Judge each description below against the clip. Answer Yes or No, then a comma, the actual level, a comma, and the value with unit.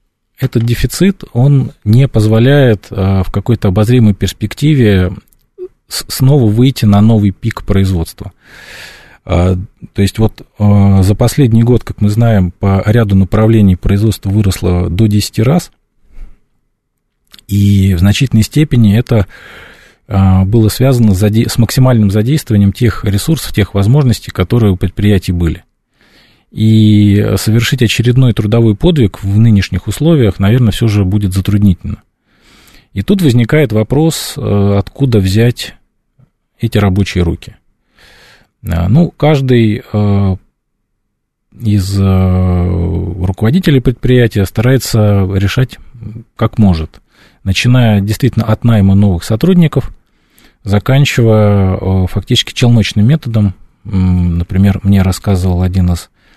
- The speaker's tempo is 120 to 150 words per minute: No, slow, 110 wpm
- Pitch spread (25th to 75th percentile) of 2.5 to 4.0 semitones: Yes, average, 3.6 semitones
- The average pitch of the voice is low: Yes, low, 105 Hz